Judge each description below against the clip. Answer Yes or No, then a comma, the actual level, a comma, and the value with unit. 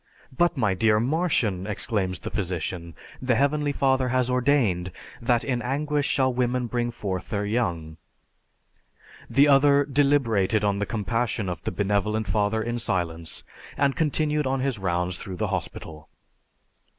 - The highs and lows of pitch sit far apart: Yes, wide, 5.7 semitones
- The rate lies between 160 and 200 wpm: No, average, 150 wpm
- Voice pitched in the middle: No, low, 115 Hz